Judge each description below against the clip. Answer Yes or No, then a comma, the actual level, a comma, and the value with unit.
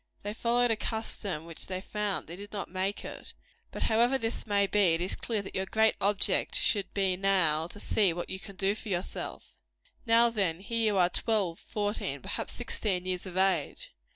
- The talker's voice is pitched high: Yes, high, 200 Hz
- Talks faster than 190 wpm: Yes, average, 200 wpm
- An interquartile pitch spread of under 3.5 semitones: Yes, average, 2.9 semitones